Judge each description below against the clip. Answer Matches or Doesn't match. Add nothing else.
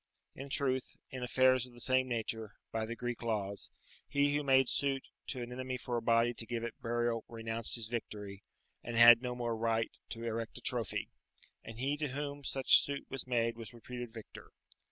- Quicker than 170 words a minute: Matches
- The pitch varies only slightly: Matches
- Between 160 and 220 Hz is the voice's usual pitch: Doesn't match